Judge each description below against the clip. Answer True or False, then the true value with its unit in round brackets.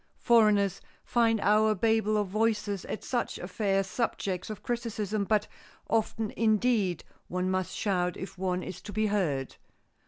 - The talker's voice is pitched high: True (210 Hz)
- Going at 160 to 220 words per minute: False (145 wpm)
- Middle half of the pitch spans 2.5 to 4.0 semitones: True (2.8 semitones)